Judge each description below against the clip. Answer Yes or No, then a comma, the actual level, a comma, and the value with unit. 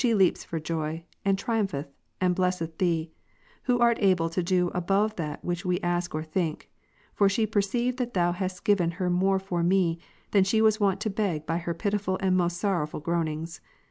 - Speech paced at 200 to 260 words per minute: Yes, fast, 205 wpm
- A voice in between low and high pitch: Yes, medium, 180 Hz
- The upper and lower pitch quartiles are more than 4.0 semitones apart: No, average, 2.9 semitones